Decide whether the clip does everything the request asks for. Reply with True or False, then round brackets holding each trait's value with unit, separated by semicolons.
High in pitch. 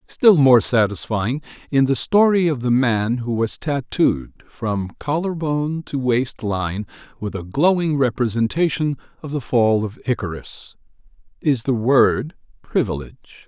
False (125 Hz)